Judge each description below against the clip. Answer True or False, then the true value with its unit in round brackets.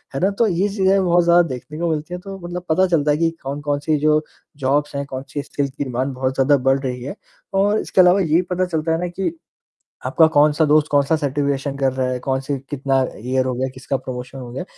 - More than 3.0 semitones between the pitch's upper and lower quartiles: True (4.4 semitones)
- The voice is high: False (145 Hz)